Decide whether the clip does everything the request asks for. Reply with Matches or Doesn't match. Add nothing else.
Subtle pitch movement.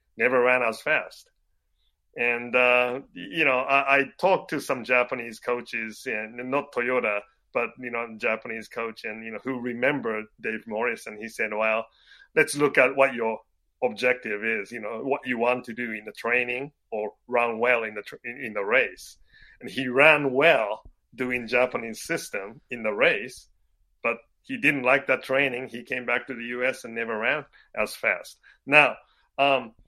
Matches